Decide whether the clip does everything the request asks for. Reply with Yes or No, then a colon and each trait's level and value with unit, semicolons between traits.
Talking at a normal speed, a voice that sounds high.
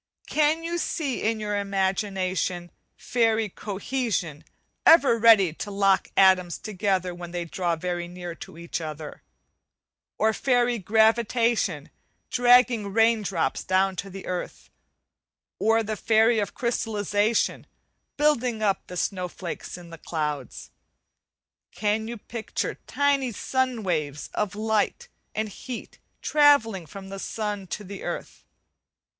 No: slow, 125 wpm; high, 205 Hz